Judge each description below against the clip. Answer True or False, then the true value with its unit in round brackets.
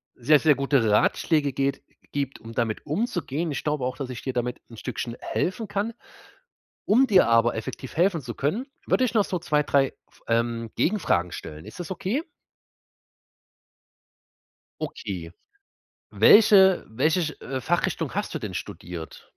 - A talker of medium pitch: True (145 Hz)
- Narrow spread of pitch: False (7.7 semitones)